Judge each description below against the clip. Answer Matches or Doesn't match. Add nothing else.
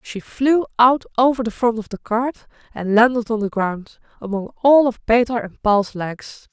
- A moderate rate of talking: Matches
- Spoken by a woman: Matches